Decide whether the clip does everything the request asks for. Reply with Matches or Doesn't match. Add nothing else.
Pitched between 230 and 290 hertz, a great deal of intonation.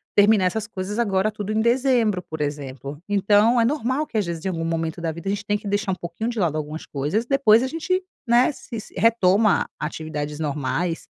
Doesn't match